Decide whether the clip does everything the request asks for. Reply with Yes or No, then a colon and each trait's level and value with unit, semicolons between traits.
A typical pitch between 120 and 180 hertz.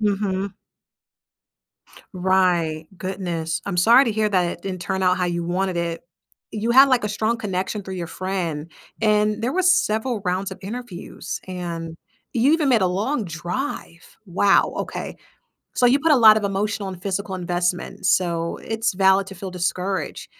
No: high, 190 Hz